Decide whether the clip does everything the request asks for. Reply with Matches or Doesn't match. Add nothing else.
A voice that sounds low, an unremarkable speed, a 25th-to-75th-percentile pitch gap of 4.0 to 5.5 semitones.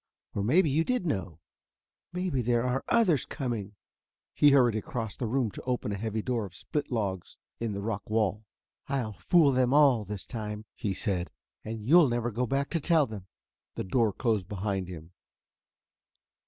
Matches